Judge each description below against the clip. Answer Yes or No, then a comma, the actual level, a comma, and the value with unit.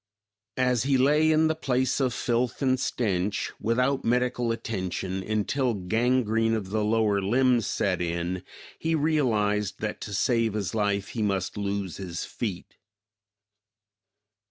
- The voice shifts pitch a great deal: No, average, 4.2 semitones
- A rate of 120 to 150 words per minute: Yes, slow, 135 wpm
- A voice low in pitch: Yes, low, 115 Hz